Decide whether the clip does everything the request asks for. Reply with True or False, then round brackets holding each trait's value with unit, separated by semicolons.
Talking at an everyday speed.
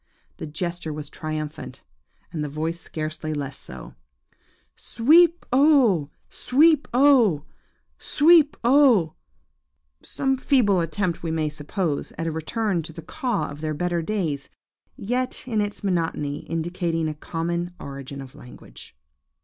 False (130 wpm)